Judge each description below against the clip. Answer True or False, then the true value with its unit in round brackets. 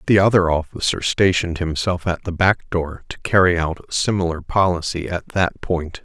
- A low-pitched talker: True (90 Hz)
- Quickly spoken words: False (180 wpm)